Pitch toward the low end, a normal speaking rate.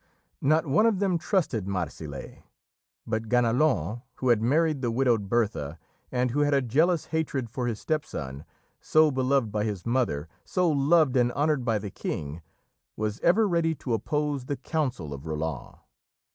Yes: low, 125 Hz; average, 165 wpm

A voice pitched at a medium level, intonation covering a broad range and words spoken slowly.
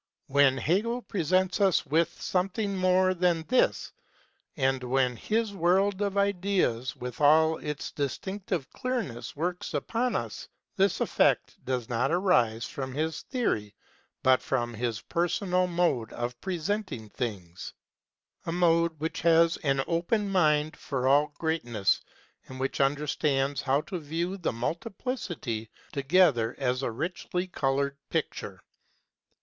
Yes: medium, 160 Hz; wide, 5.8 semitones; slow, 130 wpm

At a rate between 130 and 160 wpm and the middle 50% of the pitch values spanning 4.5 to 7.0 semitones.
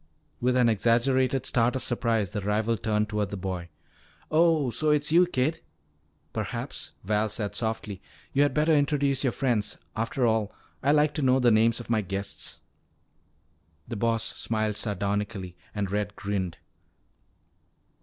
No: average, 150 wpm; average, 4.1 semitones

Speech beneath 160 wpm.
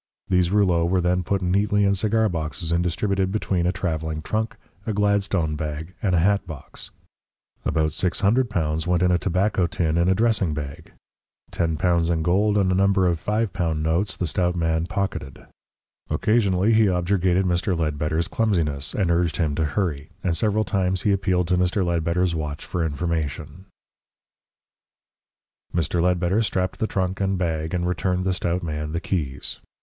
No: average, 165 wpm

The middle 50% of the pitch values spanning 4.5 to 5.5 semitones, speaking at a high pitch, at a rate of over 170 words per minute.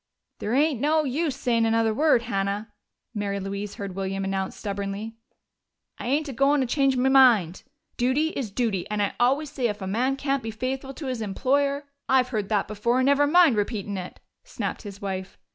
Yes: average, 5.2 semitones; high, 235 Hz; average, 195 wpm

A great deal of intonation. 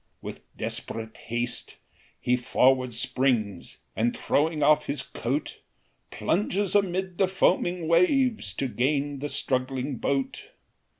Yes: wide, 5.9 semitones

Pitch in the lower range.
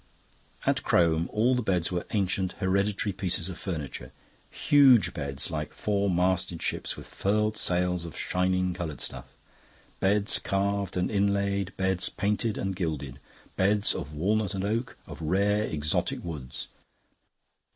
Yes: very low, 95 Hz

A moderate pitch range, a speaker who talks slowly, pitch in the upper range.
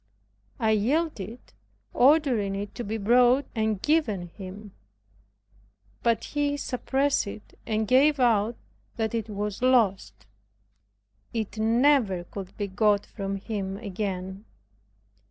Yes: average, 4.0 semitones; slow, 115 wpm; high, 220 Hz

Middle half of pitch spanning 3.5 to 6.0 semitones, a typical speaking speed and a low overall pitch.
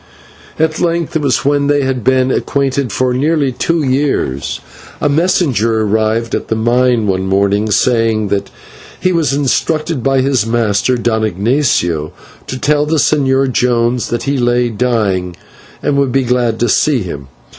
Yes: average, 4.2 semitones; average, 160 wpm; low, 125 Hz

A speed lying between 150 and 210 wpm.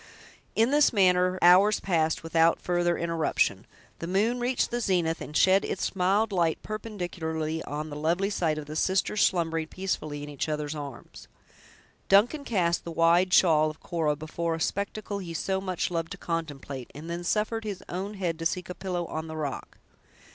Yes: average, 180 wpm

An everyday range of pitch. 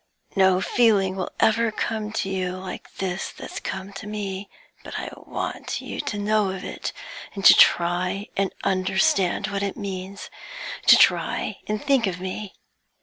No: narrow, 1.8 semitones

